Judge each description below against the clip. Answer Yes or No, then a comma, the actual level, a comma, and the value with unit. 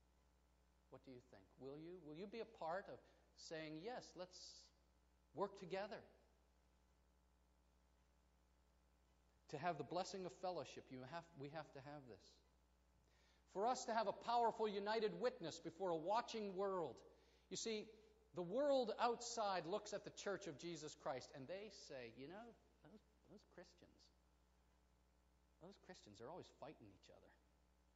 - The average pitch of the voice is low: No, medium, 145 Hz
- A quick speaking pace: No, average, 150 wpm